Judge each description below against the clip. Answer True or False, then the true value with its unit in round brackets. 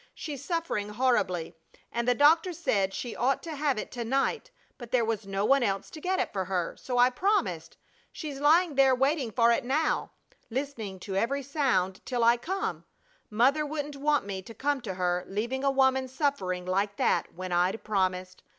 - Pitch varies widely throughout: True (6.2 semitones)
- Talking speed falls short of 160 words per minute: False (190 wpm)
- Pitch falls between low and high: False (245 Hz)